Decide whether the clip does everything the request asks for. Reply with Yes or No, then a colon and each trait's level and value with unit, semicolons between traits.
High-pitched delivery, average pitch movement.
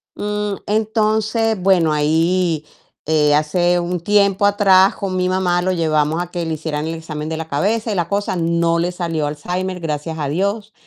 No: medium, 175 Hz; average, 3.8 semitones